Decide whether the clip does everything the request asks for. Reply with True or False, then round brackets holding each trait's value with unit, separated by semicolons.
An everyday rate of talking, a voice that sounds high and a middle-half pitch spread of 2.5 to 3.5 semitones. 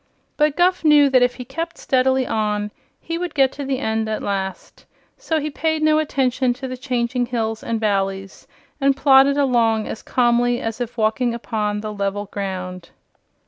False (180 wpm; 245 Hz; 4.3 semitones)